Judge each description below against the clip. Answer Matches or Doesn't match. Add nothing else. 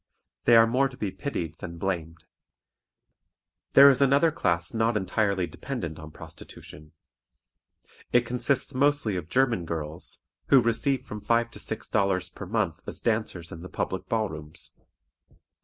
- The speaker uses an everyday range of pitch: Doesn't match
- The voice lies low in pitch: Matches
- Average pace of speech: Matches